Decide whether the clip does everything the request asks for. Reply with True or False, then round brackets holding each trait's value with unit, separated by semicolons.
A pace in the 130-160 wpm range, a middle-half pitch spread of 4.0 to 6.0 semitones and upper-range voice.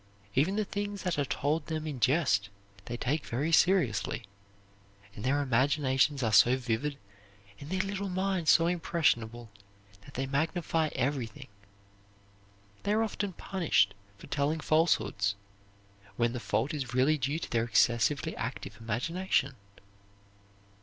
False (135 wpm; 5.6 semitones; 145 Hz)